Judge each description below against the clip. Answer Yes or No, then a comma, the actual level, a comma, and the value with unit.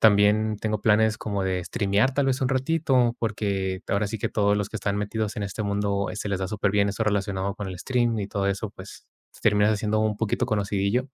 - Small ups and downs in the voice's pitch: Yes, narrow, 1.7 semitones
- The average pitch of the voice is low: Yes, low, 105 Hz